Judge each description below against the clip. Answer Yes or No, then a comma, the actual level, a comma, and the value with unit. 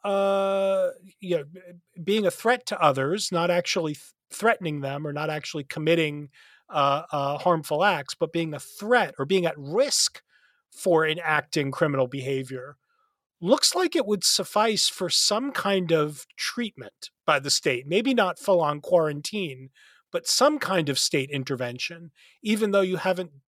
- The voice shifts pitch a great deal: Yes, wide, 5.7 semitones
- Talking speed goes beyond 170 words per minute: No, average, 155 wpm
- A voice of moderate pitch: Yes, medium, 175 Hz